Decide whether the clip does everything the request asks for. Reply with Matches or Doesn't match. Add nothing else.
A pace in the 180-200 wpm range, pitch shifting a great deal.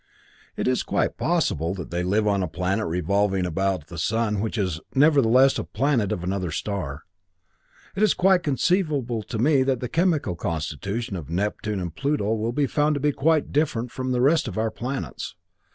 Matches